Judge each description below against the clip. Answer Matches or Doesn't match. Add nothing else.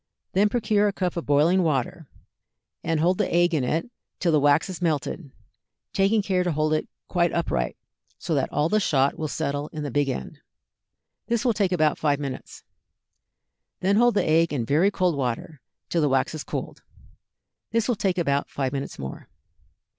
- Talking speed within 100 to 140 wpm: Doesn't match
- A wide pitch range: Doesn't match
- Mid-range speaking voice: Matches